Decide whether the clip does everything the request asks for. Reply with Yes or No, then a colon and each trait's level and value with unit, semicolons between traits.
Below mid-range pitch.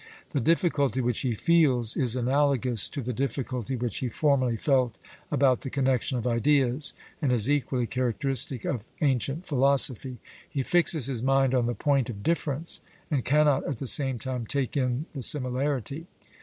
Yes: low, 130 Hz